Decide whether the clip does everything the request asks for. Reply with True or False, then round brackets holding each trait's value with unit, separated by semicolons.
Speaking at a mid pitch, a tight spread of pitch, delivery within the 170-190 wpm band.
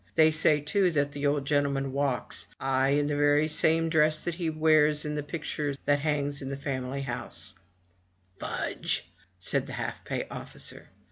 True (145 Hz; 1.8 semitones; 180 wpm)